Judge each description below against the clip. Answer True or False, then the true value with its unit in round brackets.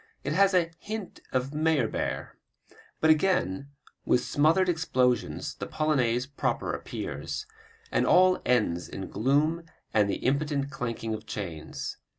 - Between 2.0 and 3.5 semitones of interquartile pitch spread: False (5.6 semitones)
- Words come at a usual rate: False (130 wpm)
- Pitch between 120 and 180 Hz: True (140 Hz)